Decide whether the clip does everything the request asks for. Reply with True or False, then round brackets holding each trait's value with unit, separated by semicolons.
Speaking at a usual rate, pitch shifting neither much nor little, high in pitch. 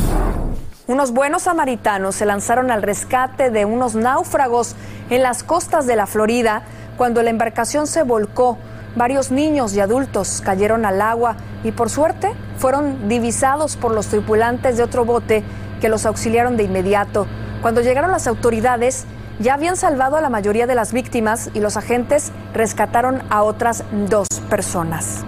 True (155 wpm; 3.4 semitones; 235 Hz)